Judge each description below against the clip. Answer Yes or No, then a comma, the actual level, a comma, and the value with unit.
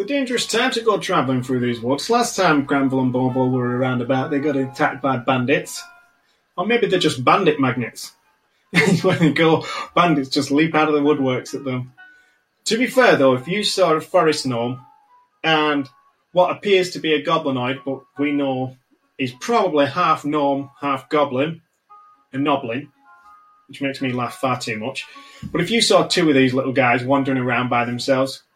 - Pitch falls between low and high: Yes, medium, 145 Hz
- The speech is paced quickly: No, average, 185 wpm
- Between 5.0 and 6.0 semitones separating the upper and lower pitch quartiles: Yes, wide, 5.6 semitones